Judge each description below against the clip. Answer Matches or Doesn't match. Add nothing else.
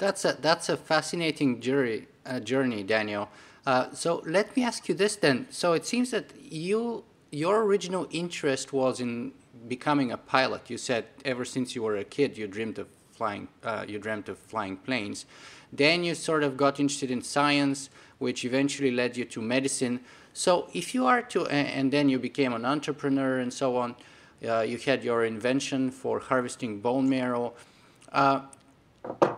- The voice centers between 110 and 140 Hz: Matches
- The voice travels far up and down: Doesn't match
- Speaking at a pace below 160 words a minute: Doesn't match